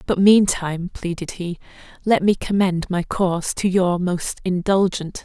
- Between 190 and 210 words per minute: No, average, 150 wpm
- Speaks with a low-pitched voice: No, medium, 185 Hz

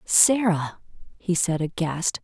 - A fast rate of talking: No, slow, 105 wpm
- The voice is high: No, medium, 175 Hz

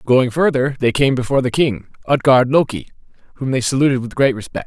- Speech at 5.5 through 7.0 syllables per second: Yes, 6.1 syllables/s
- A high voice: No, low, 130 Hz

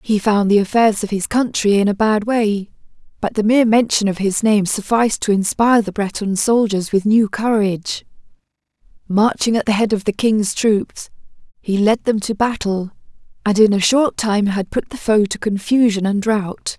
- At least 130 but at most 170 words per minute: No, average, 190 wpm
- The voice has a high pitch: Yes, high, 210 Hz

